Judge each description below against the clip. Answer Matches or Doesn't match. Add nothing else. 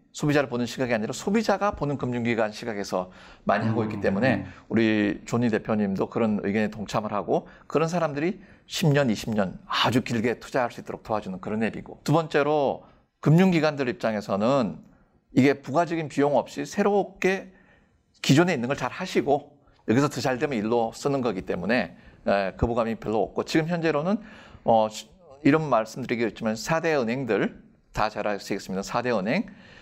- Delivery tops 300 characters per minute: Matches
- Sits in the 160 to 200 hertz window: Doesn't match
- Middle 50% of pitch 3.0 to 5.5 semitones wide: Doesn't match